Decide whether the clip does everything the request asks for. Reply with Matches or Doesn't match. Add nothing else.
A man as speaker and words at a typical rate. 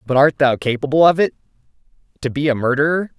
Matches